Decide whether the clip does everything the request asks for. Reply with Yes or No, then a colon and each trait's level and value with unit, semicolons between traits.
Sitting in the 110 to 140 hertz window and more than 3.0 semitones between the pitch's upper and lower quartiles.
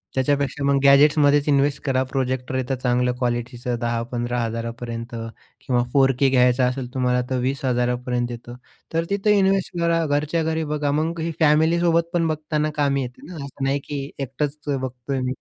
Yes: low, 135 Hz; average, 3.4 semitones